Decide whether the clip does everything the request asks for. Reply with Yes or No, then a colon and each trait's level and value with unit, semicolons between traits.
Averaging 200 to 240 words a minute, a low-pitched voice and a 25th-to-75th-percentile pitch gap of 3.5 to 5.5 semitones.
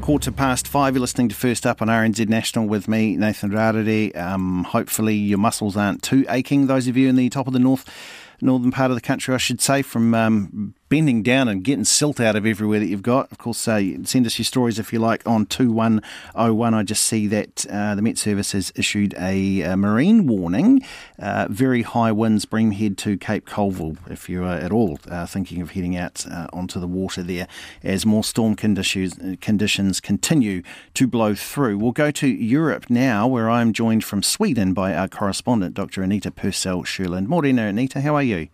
Yes: fast, 205 wpm; low, 110 Hz; average, 4.1 semitones